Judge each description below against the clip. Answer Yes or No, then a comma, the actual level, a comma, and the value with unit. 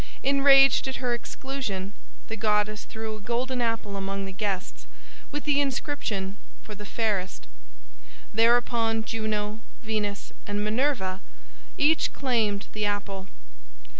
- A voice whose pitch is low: No, high, 220 Hz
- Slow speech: Yes, slow, 120 wpm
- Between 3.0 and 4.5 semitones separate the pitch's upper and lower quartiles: Yes, average, 3.4 semitones